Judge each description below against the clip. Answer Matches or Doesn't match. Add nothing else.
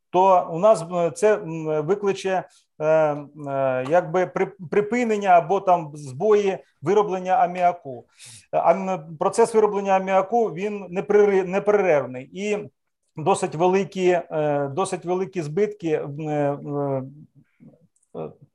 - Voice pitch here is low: Doesn't match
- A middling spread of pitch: Matches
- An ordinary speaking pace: Doesn't match